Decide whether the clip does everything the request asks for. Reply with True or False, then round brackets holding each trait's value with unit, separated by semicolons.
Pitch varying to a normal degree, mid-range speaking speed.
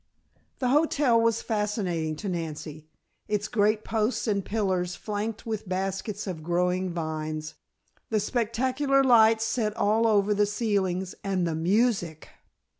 False (3.9 semitones; 130 wpm)